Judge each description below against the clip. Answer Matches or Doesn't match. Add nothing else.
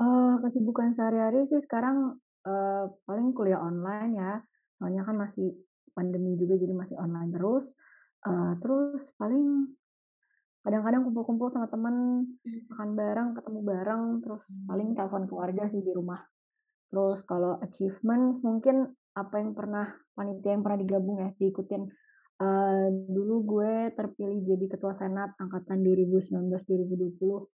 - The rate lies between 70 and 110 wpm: Doesn't match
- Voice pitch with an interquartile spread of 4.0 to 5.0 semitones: Doesn't match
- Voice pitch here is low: Doesn't match